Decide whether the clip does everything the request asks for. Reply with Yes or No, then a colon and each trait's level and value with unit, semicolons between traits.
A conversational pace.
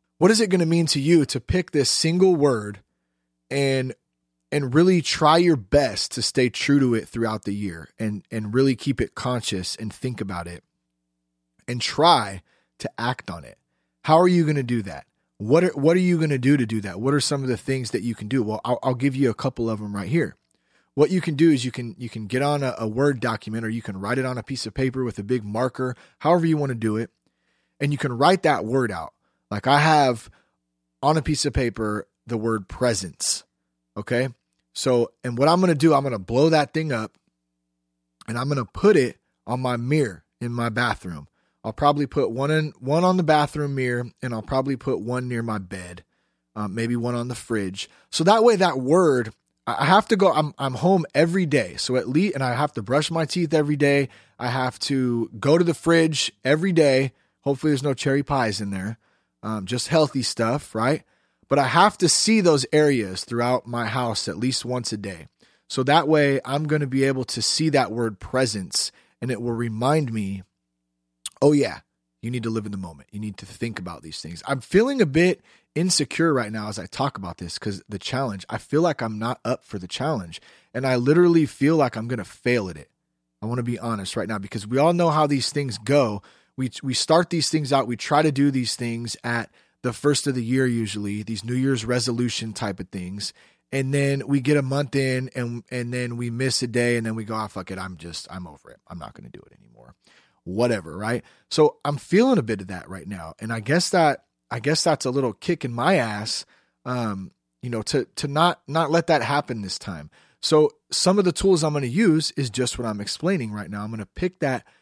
No: fast, 235 wpm